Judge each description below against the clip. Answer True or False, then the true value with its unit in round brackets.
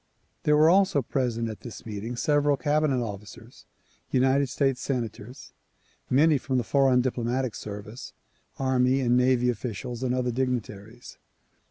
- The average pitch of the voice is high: False (125 Hz)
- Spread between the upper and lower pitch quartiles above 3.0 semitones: False (2.5 semitones)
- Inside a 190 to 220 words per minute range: False (135 wpm)